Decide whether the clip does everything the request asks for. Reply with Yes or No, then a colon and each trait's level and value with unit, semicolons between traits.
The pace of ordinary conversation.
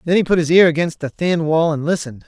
No: fast, 290 wpm